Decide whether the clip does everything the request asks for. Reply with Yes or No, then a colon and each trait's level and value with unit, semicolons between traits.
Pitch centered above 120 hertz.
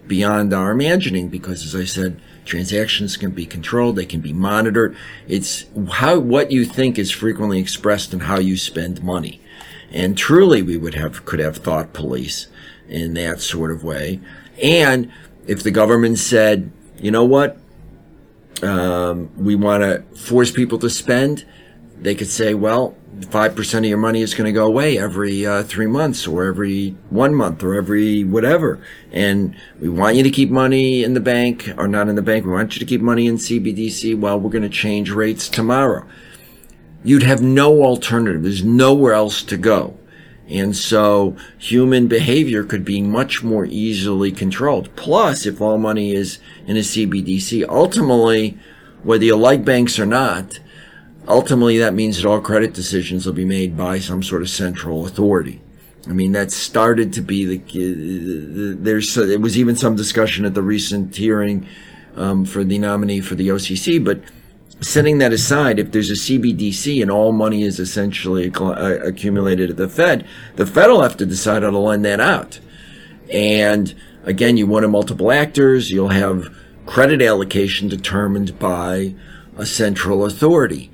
No: low, 105 Hz